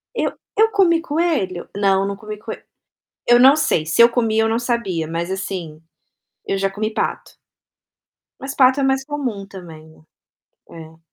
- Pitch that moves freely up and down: Yes, wide, 6.5 semitones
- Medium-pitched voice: No, high, 215 Hz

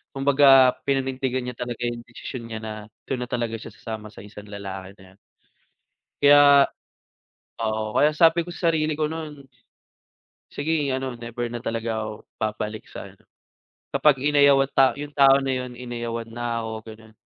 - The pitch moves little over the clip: No, average, 3.8 semitones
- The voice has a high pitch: No, low, 125 Hz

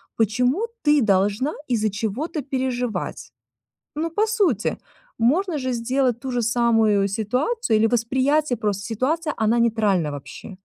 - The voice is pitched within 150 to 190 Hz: No, high, 240 Hz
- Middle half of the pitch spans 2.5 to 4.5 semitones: No, average, 4.9 semitones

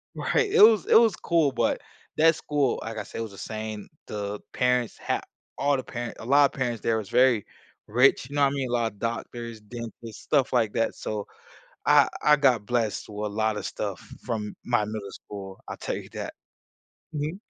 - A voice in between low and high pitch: No, low, 120 Hz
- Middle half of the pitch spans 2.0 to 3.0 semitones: No, average, 4.2 semitones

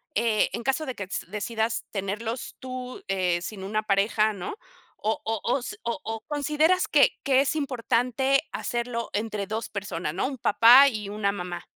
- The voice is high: Yes, high, 225 Hz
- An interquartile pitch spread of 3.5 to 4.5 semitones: Yes, average, 4.2 semitones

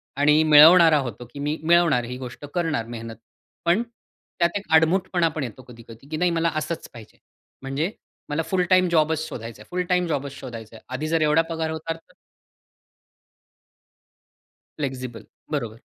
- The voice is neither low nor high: Yes, medium, 155 Hz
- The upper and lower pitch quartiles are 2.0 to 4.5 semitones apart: No, average, 4.9 semitones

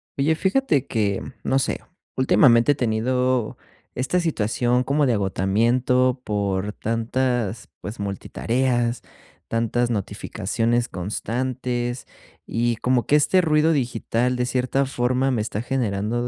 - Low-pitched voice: Yes, low, 120 Hz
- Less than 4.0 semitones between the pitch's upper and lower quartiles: Yes, narrow, 2.6 semitones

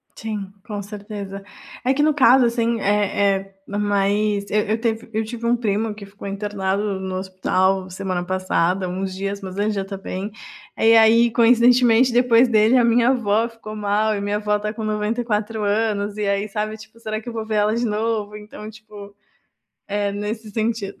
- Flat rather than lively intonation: Yes, narrow, 2.1 semitones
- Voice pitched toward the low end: No, high, 210 Hz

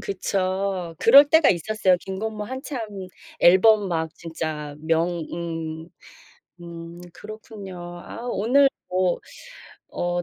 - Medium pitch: Yes, medium, 180 Hz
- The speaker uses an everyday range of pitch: Yes, average, 4.3 semitones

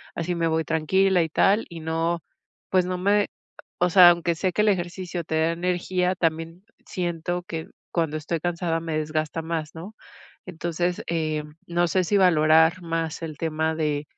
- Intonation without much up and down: Yes, narrow, 1.9 semitones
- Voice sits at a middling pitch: Yes, medium, 170 Hz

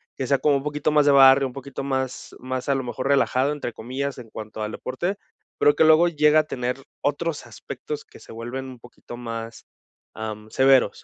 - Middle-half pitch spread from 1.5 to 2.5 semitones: No, average, 2.9 semitones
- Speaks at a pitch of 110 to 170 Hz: Yes, low, 135 Hz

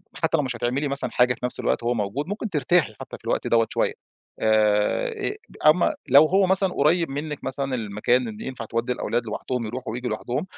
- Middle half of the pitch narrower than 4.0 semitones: No, average, 4.8 semitones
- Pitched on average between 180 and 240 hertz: No, low, 125 Hz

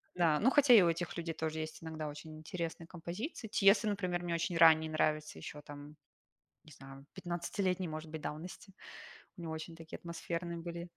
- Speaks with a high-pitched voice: No, medium, 165 Hz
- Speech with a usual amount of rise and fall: No, narrow, 2.1 semitones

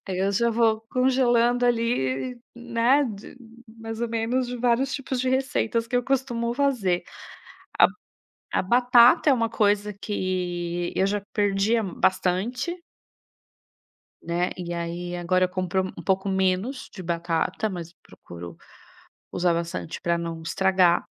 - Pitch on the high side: Yes, high, 210 Hz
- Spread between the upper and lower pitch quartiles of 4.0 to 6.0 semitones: Yes, average, 5.2 semitones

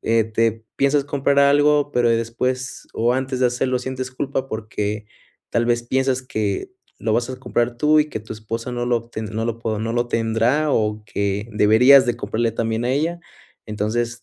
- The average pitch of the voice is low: Yes, low, 120 Hz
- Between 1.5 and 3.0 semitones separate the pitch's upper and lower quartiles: Yes, average, 2.7 semitones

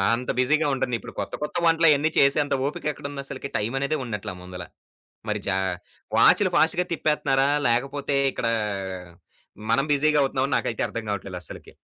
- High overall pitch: No, low, 135 Hz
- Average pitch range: Yes, average, 4.2 semitones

